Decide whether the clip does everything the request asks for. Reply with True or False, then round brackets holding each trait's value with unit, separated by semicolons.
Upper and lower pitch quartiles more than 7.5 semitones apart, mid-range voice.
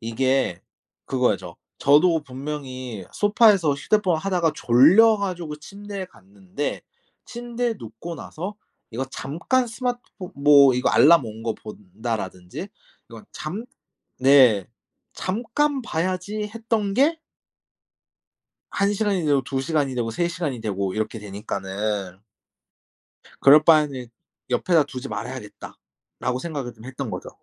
True (8.8 semitones; 145 Hz)